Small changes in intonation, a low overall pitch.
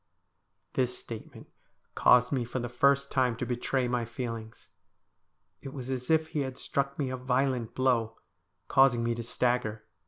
Yes: narrow, 2.0 semitones; low, 125 Hz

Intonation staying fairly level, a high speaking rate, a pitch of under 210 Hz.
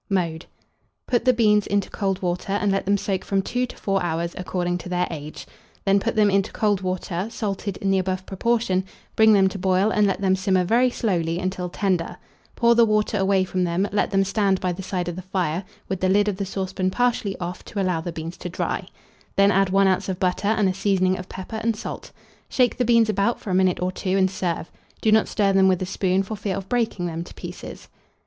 Yes: narrow, 2.0 semitones; fast, 235 wpm; high, 190 Hz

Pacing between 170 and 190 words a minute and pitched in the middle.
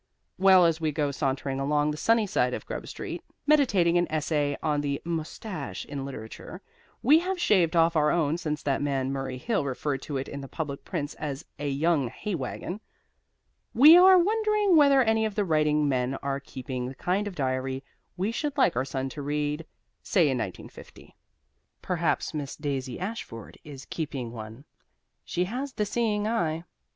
Yes: average, 180 wpm; medium, 155 Hz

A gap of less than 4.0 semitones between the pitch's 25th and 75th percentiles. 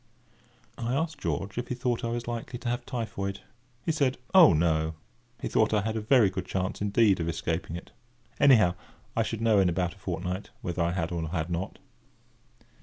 No: average, 5.2 semitones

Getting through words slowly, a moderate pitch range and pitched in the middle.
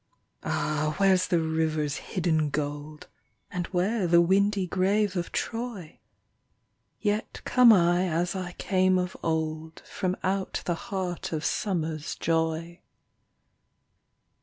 Yes: slow, 115 wpm; average, 3.1 semitones; medium, 175 Hz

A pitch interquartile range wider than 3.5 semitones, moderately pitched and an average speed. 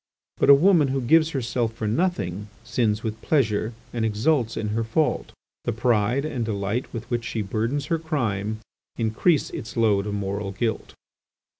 No: average, 4.3 semitones; low, 115 Hz; average, 165 wpm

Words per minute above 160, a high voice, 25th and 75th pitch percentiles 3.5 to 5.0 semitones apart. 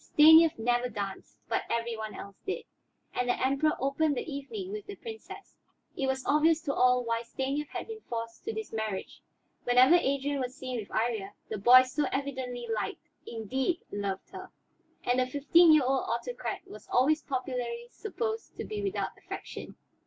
Yes: average, 175 wpm; very high, 260 Hz; average, 4.6 semitones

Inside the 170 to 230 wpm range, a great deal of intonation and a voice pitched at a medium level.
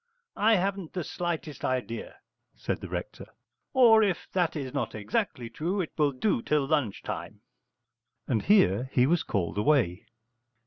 No: average, 150 wpm; wide, 7.7 semitones; medium, 145 Hz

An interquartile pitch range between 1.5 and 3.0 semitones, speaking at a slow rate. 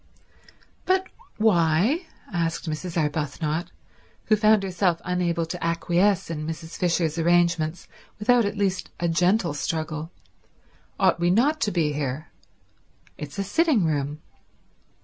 No: average, 3.8 semitones; slow, 125 wpm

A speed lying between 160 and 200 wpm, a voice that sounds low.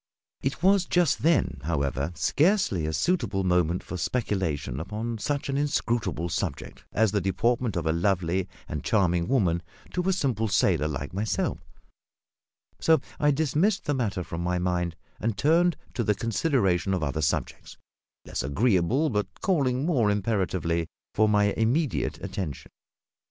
No: average, 145 wpm; low, 105 Hz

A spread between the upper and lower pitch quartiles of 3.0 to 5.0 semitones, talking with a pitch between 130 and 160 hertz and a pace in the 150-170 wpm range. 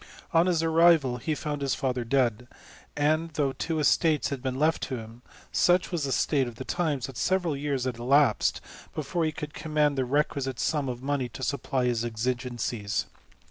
No: average, 3.6 semitones; medium, 140 Hz; average, 180 wpm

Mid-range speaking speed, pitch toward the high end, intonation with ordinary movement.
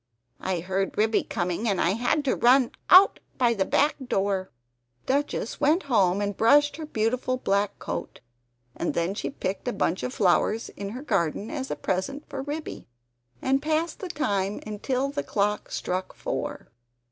No: average, 170 wpm; high, 225 Hz; wide, 6.1 semitones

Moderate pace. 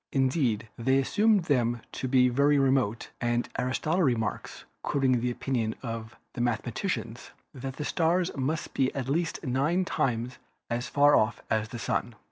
Yes: average, 160 wpm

